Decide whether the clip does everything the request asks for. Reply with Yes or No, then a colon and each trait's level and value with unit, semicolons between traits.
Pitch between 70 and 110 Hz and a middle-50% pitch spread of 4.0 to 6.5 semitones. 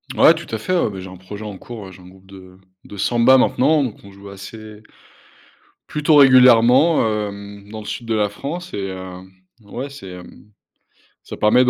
Yes: low, 105 Hz; average, 4.5 semitones